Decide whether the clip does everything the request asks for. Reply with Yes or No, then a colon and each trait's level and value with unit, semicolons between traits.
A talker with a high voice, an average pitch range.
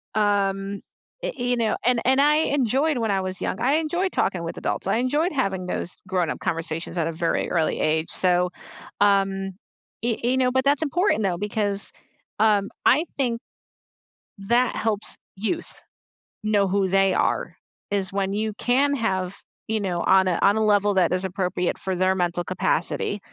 Yes: high, 200 Hz; average, 4.5 semitones